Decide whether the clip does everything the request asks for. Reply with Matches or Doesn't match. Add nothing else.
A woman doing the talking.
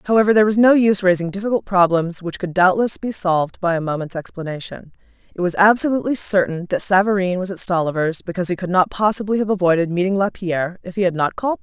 Matches